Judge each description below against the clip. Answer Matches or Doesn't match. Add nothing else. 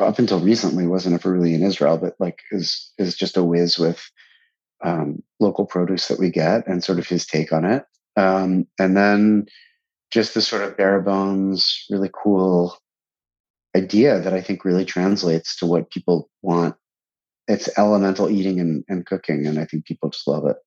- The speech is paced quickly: Doesn't match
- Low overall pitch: Matches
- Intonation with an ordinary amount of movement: Doesn't match